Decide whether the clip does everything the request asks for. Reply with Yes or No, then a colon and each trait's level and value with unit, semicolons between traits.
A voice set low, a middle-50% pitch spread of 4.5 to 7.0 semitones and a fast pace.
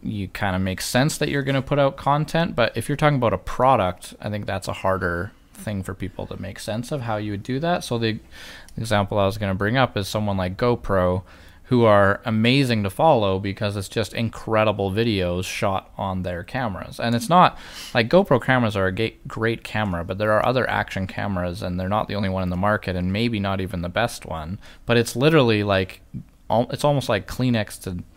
No: low, 105 Hz; average, 3.9 semitones; fast, 220 wpm